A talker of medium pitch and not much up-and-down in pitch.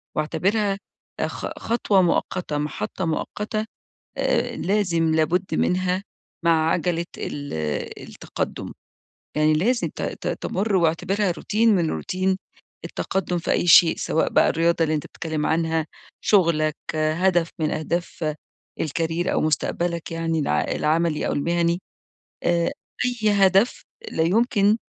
No: medium, 170 Hz; average, 3.1 semitones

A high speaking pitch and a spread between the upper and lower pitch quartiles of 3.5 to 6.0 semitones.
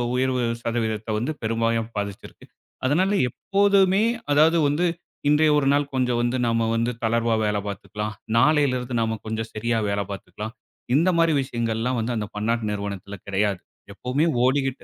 No: low, 115 Hz; average, 4.4 semitones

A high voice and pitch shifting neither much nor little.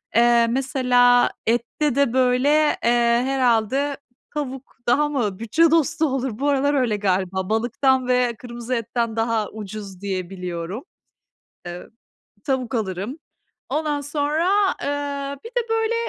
Yes: very high, 250 Hz; average, 4.2 semitones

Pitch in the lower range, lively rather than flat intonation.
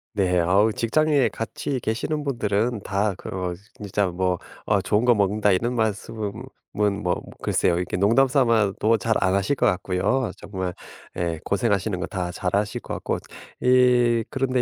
No: low, 105 Hz; average, 4.0 semitones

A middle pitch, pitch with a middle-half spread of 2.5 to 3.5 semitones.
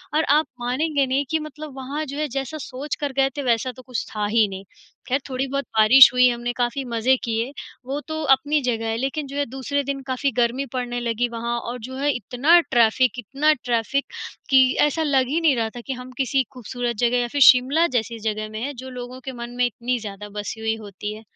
No: very high, 255 Hz; average, 2.8 semitones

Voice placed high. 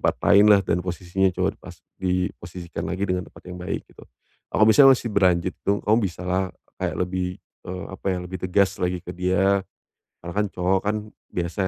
No: very low, 90 Hz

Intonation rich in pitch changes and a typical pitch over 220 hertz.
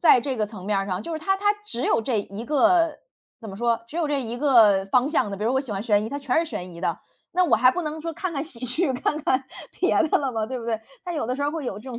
Yes: wide, 5.7 semitones; very high, 255 Hz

